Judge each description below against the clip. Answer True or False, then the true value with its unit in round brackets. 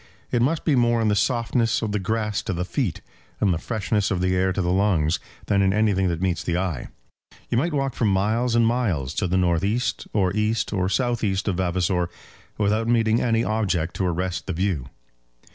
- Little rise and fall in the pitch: False (3.8 semitones)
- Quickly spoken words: True (210 wpm)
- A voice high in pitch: False (100 Hz)